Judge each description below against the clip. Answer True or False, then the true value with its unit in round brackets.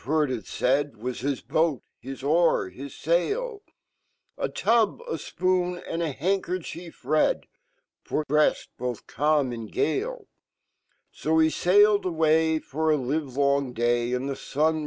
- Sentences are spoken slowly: True (130 wpm)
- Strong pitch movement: False (4.7 semitones)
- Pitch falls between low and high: True (155 Hz)